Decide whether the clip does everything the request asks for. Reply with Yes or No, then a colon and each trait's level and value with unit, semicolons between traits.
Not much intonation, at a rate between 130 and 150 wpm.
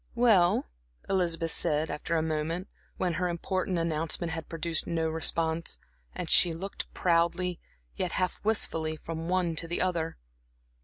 Yes: narrow, 1.9 semitones; average, 145 wpm